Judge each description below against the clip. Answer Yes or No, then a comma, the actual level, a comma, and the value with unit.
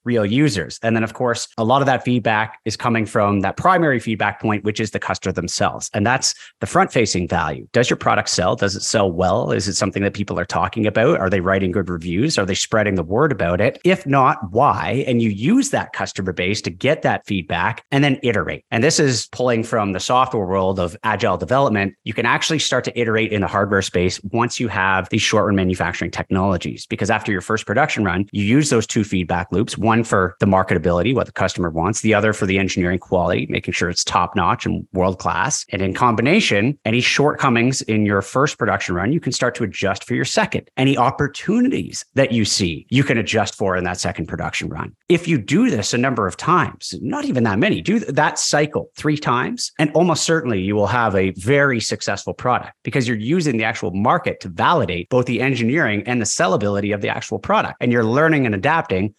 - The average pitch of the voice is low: Yes, low, 110 Hz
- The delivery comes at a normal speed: No, fast, 220 wpm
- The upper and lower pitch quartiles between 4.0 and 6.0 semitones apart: Yes, average, 4.5 semitones